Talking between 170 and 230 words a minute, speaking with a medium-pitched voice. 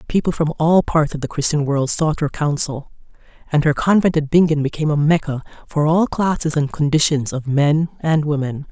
Yes: average, 195 wpm; medium, 150 Hz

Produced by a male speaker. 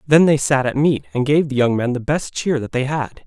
Yes: male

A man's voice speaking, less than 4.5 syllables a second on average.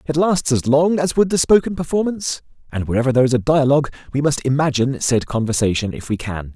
No: male; 6.4 syllables/s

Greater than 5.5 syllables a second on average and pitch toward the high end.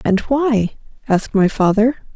No: 4.5 syllables/s; high, 220 Hz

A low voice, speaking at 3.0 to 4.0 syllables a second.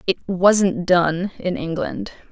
No: medium, 185 Hz; 3.6 syllables/s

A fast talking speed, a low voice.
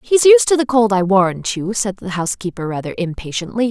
No: fast, 210 wpm; high, 205 Hz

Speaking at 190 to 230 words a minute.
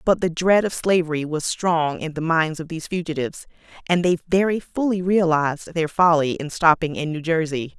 Yes: average, 195 wpm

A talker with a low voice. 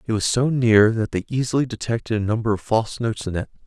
Yes: low, 115 Hz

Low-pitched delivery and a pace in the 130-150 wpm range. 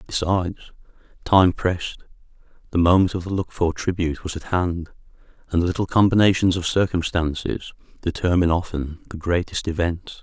Yes: very low, 90 Hz; slow, 135 wpm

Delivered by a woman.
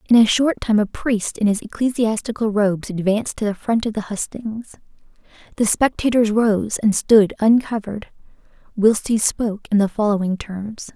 Yes: female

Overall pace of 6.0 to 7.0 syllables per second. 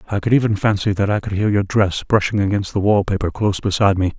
Yes: 6.6 syllables/s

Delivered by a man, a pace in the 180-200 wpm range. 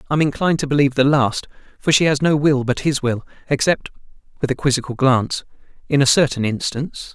Yes: male; average, 185 wpm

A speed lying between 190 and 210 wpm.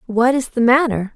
Yes: fast, 205 wpm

